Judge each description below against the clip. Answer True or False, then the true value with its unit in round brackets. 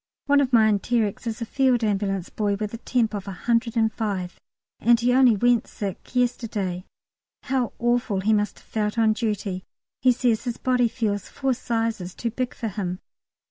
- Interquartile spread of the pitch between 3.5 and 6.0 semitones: False (3.0 semitones)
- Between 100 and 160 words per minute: False (175 wpm)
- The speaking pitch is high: True (225 Hz)